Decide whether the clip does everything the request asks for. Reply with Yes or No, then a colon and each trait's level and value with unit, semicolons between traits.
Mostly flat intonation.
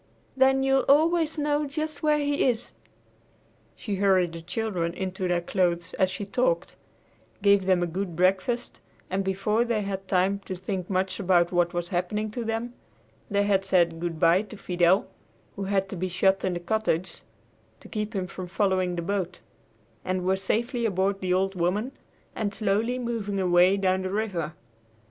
No: average, 3.2 semitones